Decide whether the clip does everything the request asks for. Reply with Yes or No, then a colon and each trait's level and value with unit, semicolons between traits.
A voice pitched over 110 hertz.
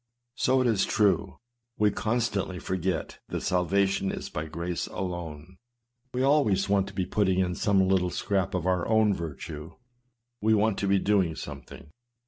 No: very low, 95 Hz